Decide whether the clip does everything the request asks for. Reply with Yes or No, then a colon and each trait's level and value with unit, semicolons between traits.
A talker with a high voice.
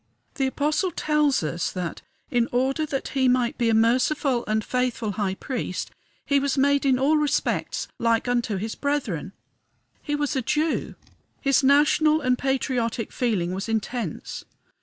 Yes: very high, 255 Hz